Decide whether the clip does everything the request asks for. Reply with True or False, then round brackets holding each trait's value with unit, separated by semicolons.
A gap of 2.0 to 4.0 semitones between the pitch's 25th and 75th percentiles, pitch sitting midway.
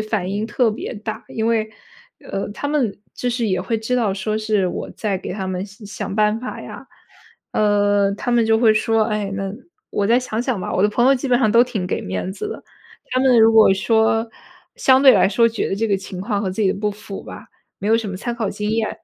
False (2.6 semitones; 215 Hz)